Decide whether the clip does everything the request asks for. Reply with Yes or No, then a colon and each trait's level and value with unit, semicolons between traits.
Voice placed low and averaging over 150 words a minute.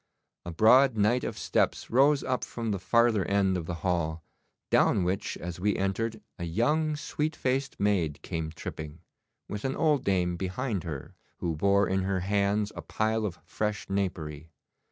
Yes: low, 100 Hz; average, 170 wpm